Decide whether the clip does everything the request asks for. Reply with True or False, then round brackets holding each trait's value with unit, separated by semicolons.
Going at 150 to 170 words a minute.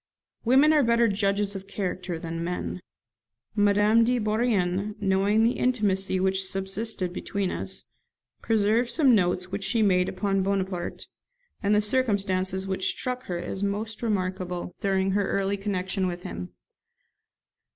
False (140 wpm)